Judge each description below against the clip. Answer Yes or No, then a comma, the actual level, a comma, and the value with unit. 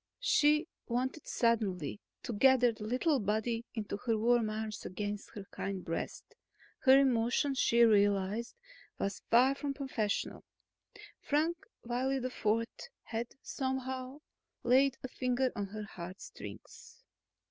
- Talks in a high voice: Yes, high, 235 Hz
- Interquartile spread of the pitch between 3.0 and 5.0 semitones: Yes, average, 3.8 semitones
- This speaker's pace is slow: Yes, slow, 120 wpm